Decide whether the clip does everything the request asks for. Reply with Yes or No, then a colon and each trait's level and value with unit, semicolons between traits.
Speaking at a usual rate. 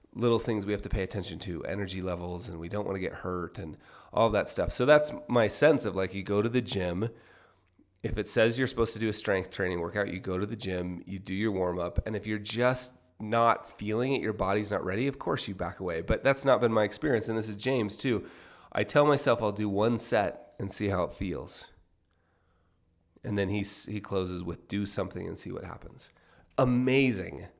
No: fast, 230 wpm